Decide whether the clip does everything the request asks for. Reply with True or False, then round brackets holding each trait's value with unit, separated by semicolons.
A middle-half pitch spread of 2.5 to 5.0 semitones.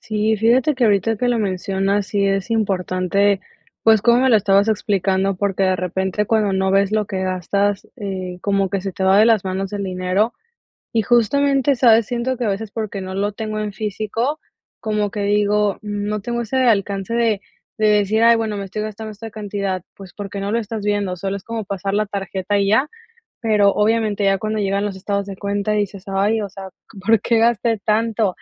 False (2.1 semitones)